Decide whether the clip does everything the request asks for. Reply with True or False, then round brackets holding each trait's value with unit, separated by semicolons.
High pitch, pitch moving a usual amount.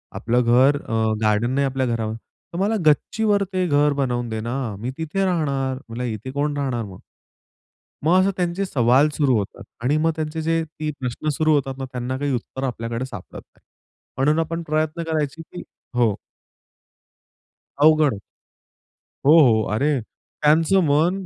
False (140 Hz; 4.4 semitones)